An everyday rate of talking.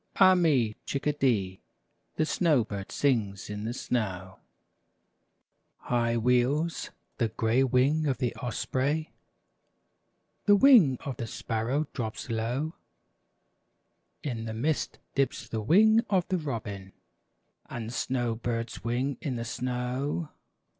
No: slow, 125 wpm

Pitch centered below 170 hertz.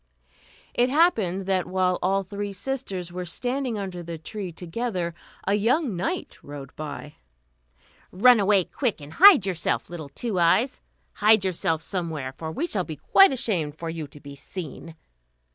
No: medium, 185 Hz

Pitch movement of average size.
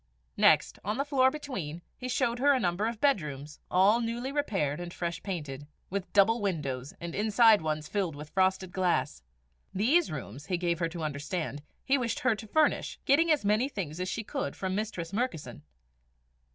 No: wide, 6.6 semitones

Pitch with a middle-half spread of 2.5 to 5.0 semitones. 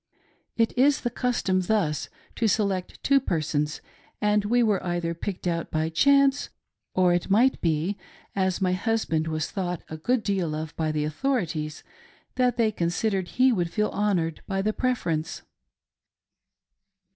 No: wide, 5.4 semitones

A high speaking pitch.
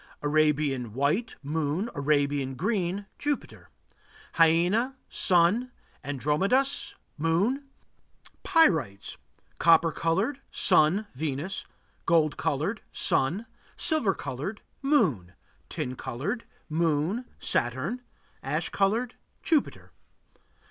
No: medium, 165 Hz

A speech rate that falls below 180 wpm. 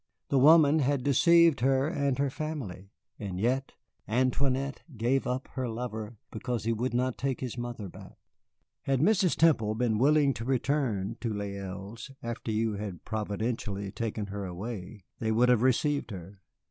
Yes: average, 160 wpm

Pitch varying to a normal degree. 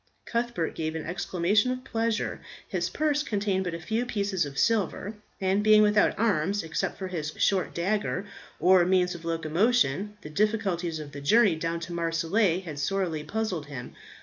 Yes: average, 4.3 semitones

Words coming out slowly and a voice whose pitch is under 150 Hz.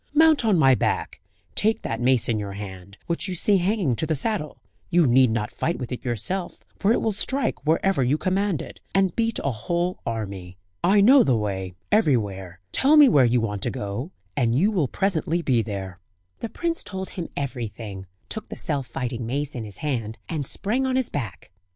No: average, 200 wpm; medium, 140 Hz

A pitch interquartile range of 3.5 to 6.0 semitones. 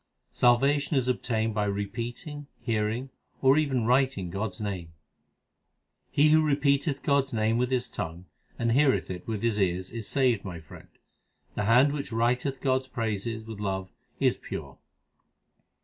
Yes: average, 4.5 semitones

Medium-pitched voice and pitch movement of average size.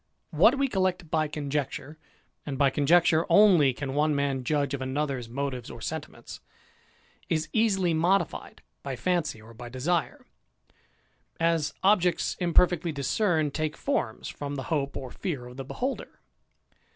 Yes: medium, 150 Hz; average, 4.4 semitones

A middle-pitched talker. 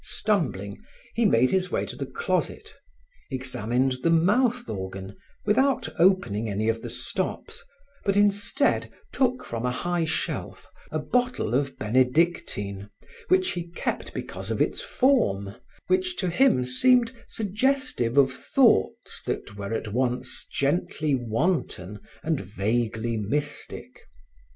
Yes: medium, 145 Hz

